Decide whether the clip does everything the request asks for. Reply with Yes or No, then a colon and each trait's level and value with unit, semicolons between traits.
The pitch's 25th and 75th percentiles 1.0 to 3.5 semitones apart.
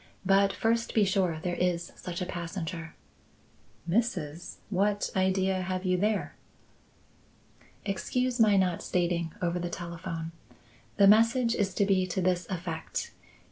Yes: narrow, 2.6 semitones